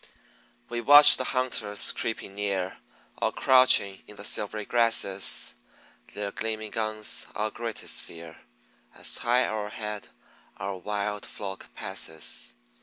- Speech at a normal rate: No, slow, 115 wpm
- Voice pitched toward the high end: No, low, 105 Hz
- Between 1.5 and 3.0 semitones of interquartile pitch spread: Yes, narrow, 2.4 semitones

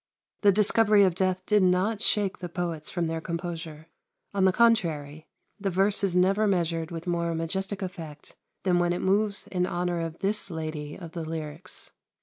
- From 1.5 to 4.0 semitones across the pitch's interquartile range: Yes, average, 3.0 semitones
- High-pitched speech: No, medium, 180 Hz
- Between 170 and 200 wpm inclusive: Yes, average, 175 wpm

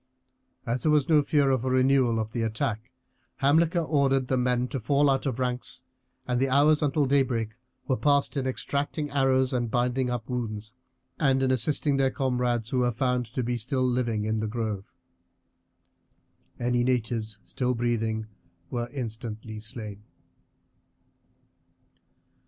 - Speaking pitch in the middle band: No, low, 125 Hz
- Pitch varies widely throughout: No, average, 2.7 semitones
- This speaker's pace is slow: No, average, 150 wpm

